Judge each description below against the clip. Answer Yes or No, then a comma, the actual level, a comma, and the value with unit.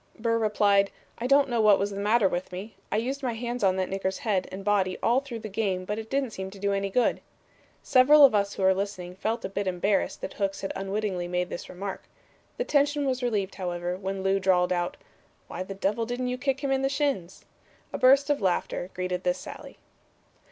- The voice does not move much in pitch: No, average, 4.3 semitones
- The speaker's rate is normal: No, fast, 220 wpm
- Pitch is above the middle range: Yes, high, 200 Hz